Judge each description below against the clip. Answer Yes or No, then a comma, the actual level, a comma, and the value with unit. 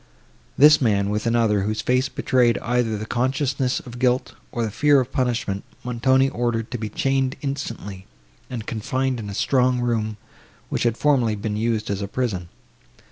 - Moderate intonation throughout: Yes, average, 3.1 semitones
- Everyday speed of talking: Yes, average, 170 wpm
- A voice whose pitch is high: No, low, 120 Hz